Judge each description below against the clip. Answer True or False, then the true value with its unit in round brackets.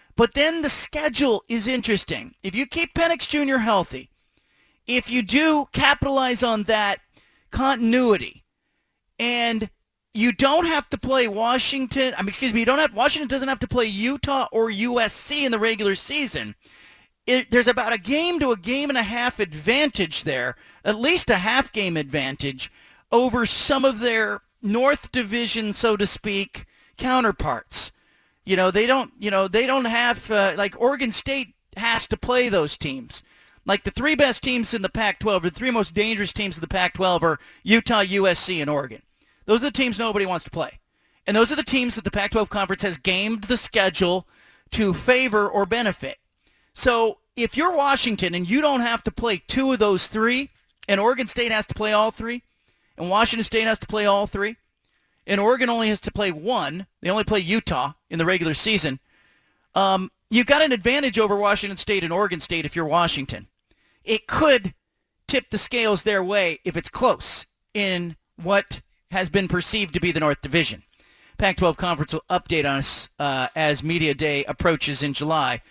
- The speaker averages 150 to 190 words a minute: True (180 wpm)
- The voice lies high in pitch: True (215 Hz)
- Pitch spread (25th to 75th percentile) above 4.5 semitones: True (5.1 semitones)